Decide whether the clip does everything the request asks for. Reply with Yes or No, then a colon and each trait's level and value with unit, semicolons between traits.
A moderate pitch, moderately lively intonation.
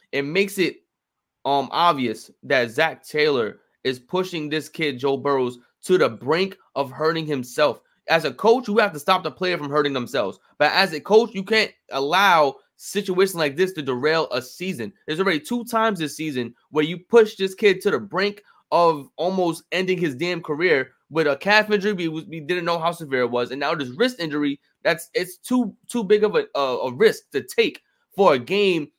No: medium, 175 Hz; wide, 5.7 semitones